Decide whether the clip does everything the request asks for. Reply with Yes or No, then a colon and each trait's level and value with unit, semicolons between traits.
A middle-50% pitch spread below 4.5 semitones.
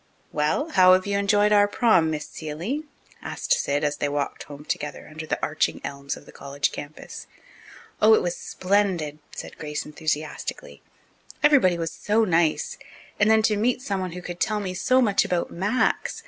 No: wide, 5.6 semitones